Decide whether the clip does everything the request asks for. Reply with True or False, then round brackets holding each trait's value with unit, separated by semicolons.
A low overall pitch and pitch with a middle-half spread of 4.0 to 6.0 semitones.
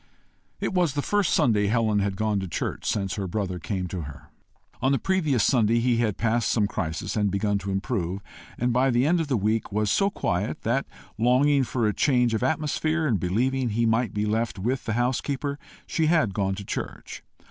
True (115 Hz; 4.7 semitones)